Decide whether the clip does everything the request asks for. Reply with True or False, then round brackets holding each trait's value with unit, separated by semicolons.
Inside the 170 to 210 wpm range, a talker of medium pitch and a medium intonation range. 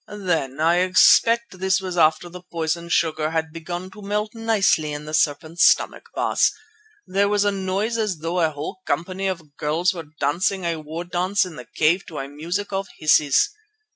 True (175 wpm; 175 Hz; 3.7 semitones)